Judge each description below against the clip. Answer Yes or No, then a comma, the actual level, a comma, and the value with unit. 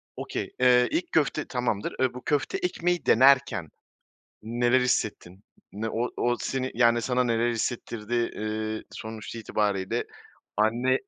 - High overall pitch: No, low, 120 Hz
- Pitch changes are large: No, average, 2.7 semitones